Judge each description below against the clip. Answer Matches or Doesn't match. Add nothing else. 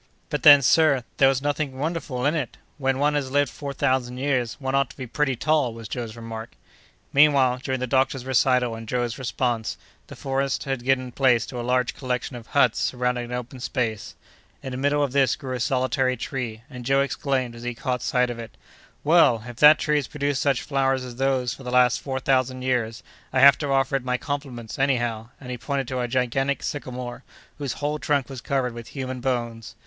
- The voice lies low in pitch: Matches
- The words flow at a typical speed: Doesn't match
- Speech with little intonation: Matches